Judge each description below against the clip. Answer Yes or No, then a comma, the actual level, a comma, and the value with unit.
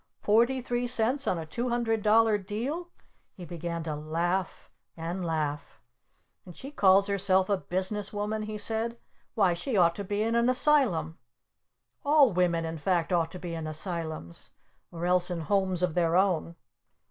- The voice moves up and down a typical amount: Yes, average, 4.7 semitones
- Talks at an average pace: Yes, average, 170 wpm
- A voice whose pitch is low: No, high, 190 Hz